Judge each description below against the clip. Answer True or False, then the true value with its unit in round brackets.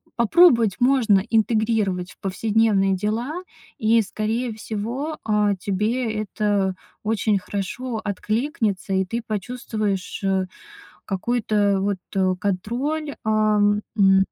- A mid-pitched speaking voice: False (215 Hz)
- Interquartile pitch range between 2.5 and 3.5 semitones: True (2.9 semitones)